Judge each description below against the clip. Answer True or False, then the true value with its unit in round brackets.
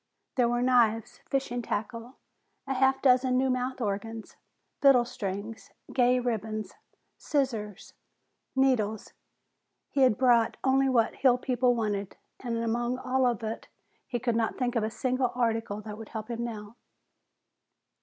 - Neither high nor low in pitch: False (240 Hz)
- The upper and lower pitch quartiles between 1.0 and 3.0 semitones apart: True (2.4 semitones)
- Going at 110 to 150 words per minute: True (145 wpm)